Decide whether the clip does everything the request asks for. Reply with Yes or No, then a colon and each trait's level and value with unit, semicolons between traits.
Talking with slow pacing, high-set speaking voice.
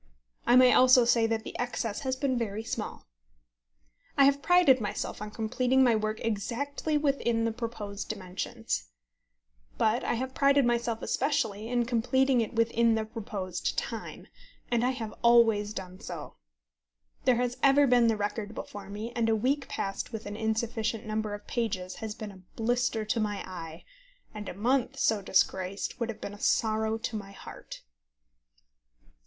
No: average, 165 wpm; high, 225 Hz